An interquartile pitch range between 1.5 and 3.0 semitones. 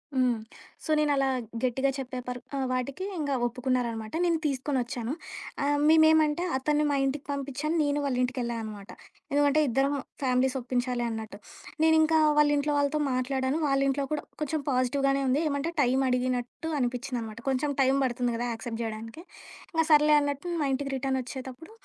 Yes: average, 2.7 semitones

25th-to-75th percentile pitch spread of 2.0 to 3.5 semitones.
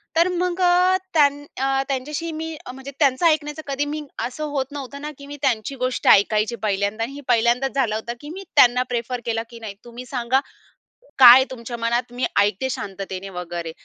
No: average, 3.9 semitones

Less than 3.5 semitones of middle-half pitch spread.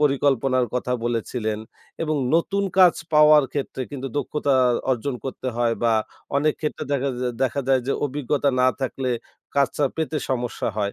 Yes: average, 2.9 semitones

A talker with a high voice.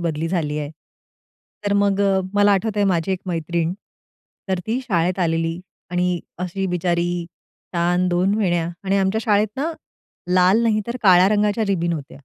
No: medium, 180 Hz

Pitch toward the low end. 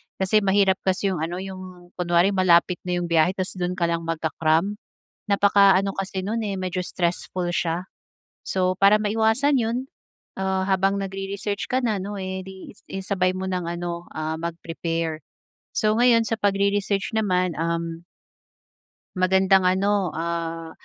No: high, 190 Hz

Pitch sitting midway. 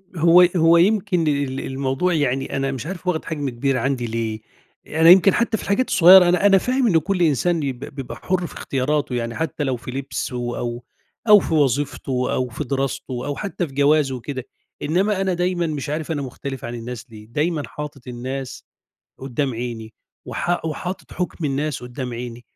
Yes: medium, 145 Hz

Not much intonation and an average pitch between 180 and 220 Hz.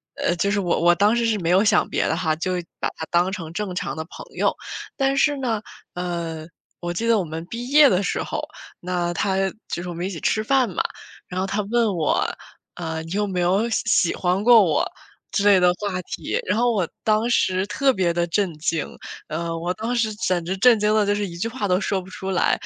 No: average, 3.8 semitones; high, 190 Hz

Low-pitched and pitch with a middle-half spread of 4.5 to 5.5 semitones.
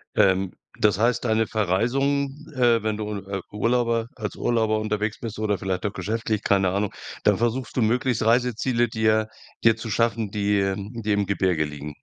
No: low, 110 Hz; narrow, 2.5 semitones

